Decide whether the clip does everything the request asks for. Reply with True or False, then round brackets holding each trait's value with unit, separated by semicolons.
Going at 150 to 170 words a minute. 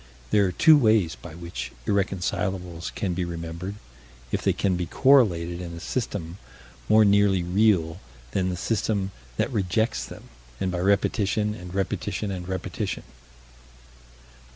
False (140 wpm)